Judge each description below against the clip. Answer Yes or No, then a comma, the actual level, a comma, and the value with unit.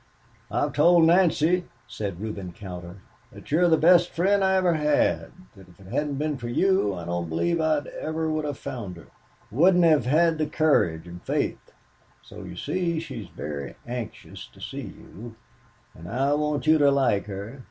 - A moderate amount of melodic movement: No, wide, 8.6 semitones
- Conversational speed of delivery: Yes, average, 185 wpm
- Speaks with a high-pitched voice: No, medium, 145 Hz